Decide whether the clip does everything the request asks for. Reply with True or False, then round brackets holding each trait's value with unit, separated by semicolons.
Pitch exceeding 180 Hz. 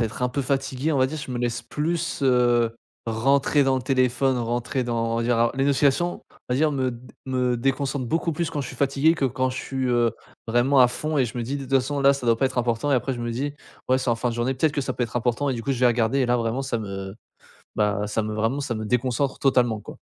False (125 Hz)